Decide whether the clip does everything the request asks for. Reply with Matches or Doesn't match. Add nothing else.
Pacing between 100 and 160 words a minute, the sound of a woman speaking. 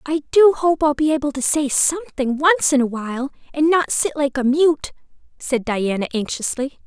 Doesn't match